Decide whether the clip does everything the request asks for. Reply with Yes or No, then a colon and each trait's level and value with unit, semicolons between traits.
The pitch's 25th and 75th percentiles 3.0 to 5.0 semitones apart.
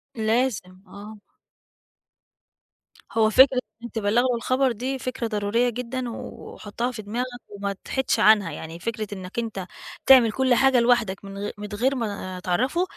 Yes: average, 3.6 semitones